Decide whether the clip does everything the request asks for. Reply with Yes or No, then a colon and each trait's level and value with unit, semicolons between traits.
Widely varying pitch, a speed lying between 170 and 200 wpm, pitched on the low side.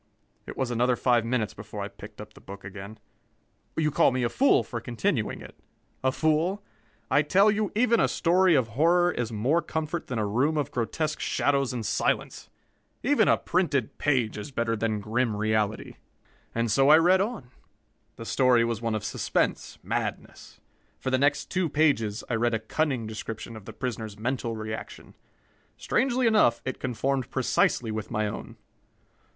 Yes: wide, 5.8 semitones; average, 175 wpm; low, 125 Hz